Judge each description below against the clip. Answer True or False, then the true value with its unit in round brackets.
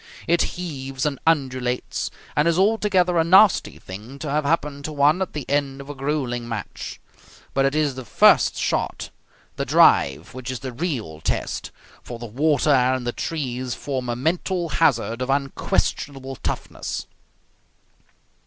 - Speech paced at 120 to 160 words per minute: True (155 wpm)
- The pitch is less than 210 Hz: True (140 Hz)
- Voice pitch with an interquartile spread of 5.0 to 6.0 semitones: False (3.6 semitones)